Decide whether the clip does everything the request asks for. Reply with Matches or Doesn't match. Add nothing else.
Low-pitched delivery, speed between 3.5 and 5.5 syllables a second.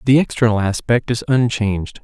Matches